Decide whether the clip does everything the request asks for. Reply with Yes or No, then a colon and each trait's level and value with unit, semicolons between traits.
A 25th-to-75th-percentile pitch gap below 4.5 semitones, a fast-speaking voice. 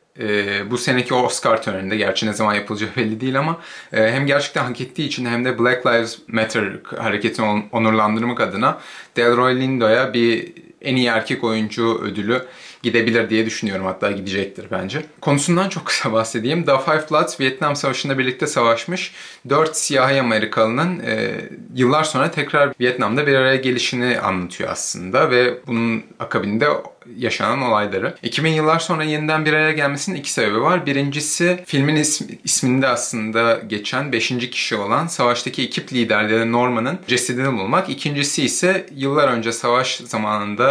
Yes: average, 4.0 semitones; fast, 150 wpm